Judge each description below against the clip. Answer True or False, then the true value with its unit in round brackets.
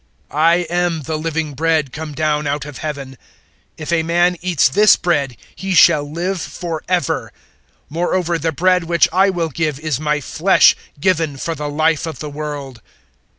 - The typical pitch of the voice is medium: True (160 Hz)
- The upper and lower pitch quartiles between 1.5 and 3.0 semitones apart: True (2.7 semitones)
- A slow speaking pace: False (175 wpm)